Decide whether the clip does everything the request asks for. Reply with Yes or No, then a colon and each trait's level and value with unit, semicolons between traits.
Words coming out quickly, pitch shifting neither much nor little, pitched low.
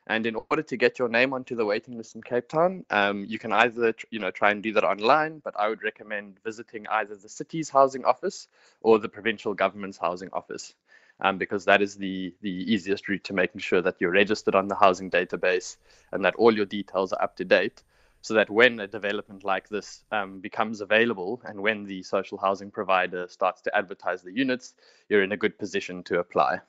Yes: fast, 220 wpm; average, 3.2 semitones; low, 105 Hz